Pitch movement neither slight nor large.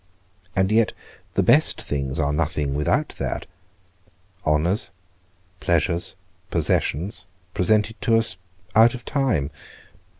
No: wide, 6.7 semitones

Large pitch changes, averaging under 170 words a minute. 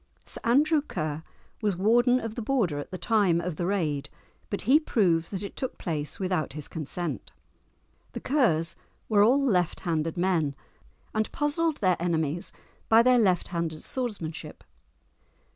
Yes: wide, 6.3 semitones; average, 155 wpm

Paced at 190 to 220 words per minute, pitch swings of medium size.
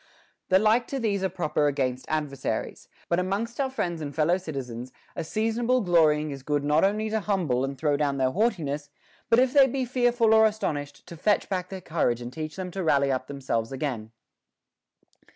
No: average, 195 wpm; wide, 7.3 semitones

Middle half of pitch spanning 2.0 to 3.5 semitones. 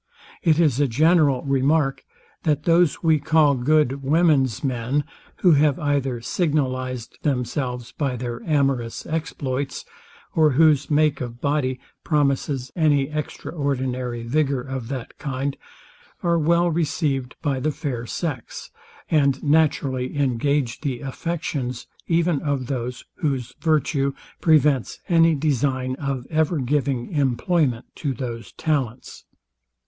Yes: average, 3.1 semitones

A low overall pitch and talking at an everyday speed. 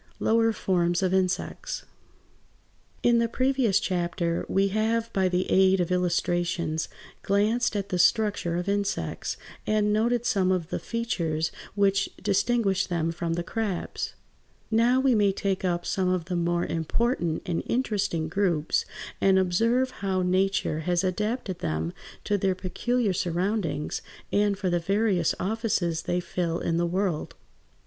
No: high, 190 Hz; average, 145 wpm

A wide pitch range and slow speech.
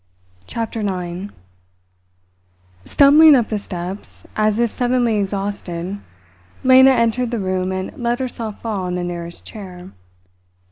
No: average, 4.4 semitones; slow, 125 wpm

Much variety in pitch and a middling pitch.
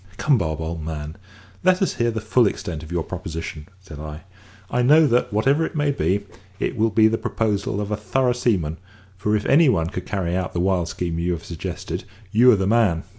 No: wide, 5.9 semitones; low, 100 Hz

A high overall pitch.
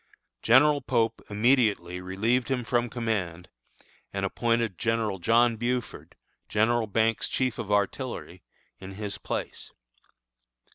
No: low, 115 Hz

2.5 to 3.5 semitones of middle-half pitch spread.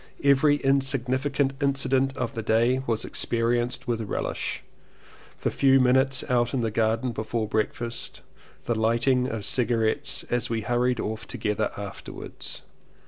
Yes: average, 2.9 semitones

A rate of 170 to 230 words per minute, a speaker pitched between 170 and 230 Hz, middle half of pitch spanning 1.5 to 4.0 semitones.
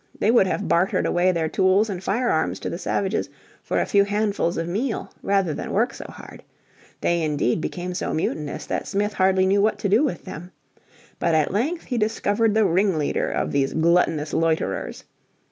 Yes: average, 185 wpm; high, 190 Hz; average, 3.7 semitones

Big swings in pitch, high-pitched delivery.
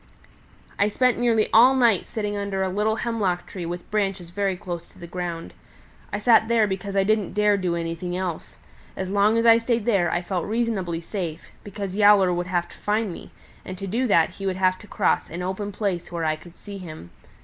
No: average, 3.1 semitones; high, 195 Hz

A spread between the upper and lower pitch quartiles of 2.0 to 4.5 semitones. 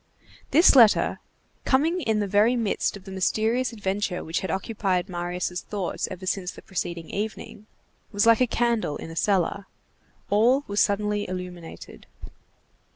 Yes: average, 3.6 semitones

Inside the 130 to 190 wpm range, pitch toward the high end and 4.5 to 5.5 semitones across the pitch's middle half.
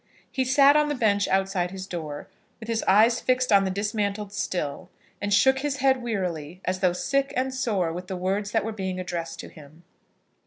No: average, 200 wpm; high, 200 Hz; average, 5.2 semitones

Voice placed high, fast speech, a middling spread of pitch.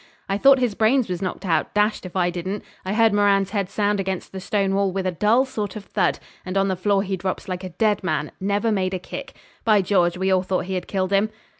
No: high, 195 Hz; fast, 255 wpm; narrow, 2.0 semitones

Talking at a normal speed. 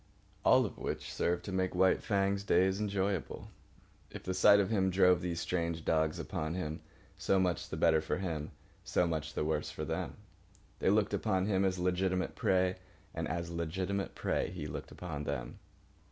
Yes: average, 180 wpm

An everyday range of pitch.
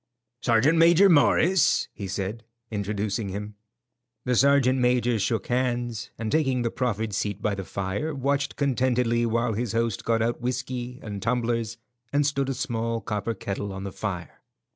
Yes: average, 3.5 semitones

